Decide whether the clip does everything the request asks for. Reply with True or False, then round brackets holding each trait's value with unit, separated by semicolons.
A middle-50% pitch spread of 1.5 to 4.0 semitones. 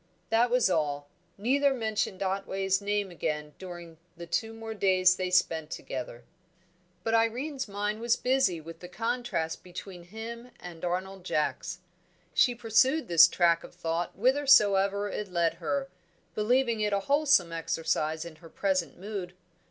False (4.8 semitones)